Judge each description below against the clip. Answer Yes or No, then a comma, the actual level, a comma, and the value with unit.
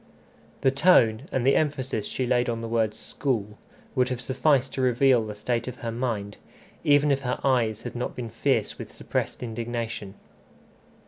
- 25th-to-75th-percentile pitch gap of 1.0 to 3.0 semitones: Yes, average, 2.7 semitones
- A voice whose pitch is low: Yes, low, 120 Hz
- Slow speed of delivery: No, average, 175 wpm